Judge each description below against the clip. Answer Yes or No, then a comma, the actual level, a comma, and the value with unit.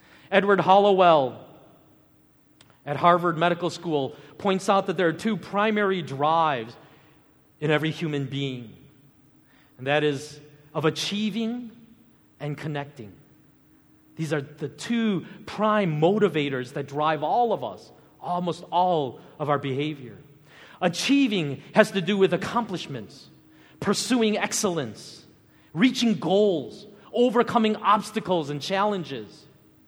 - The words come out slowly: Yes, slow, 110 wpm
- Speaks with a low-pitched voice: No, medium, 165 Hz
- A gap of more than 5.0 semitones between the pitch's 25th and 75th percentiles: Yes, wide, 5.6 semitones